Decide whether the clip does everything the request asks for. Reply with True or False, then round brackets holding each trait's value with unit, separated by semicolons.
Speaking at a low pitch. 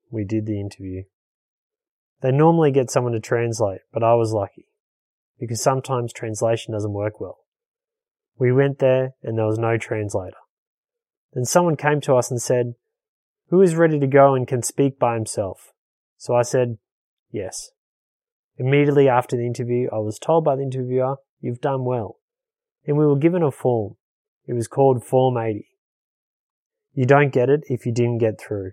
True (130 Hz)